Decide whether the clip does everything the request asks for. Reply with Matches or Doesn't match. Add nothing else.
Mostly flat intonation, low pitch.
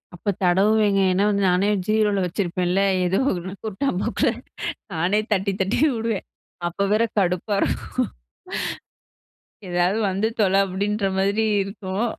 Doesn't match